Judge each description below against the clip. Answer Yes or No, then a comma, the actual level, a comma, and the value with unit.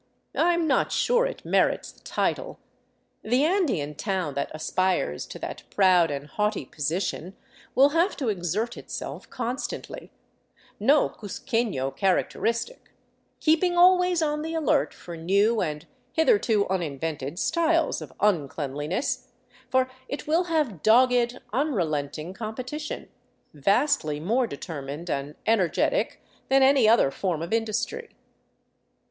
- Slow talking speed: Yes, slow, 130 wpm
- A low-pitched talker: No, high, 220 Hz